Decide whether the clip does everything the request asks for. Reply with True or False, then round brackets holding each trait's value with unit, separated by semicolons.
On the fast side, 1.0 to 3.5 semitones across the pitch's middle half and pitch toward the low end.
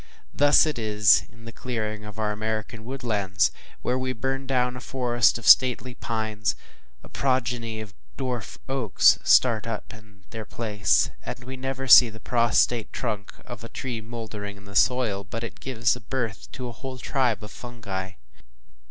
False (165 wpm; 2.9 semitones; 115 Hz)